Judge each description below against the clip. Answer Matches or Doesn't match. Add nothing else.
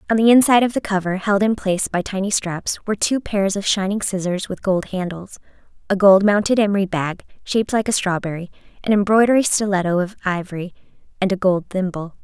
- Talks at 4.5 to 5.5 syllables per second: Doesn't match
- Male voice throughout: Doesn't match